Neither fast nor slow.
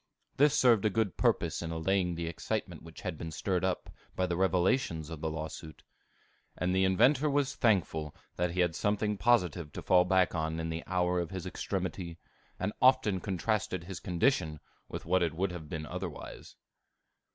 Yes: average, 180 wpm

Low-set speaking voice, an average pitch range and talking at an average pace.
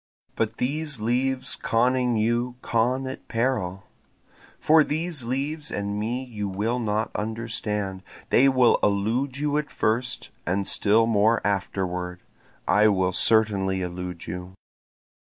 No: low, 115 Hz; average, 4.2 semitones; slow, 125 wpm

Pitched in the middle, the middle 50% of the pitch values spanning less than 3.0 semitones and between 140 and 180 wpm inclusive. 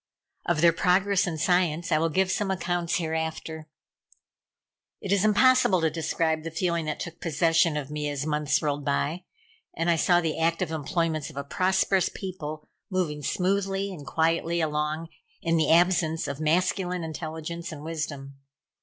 Yes: medium, 165 Hz; narrow, 2.6 semitones; average, 160 wpm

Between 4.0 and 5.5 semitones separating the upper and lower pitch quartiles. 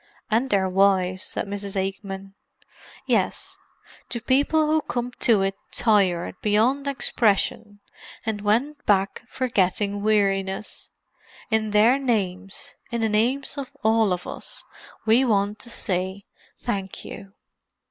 No: average, 3.4 semitones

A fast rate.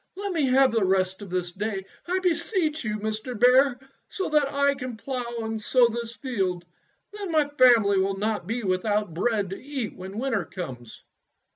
No: average, 180 wpm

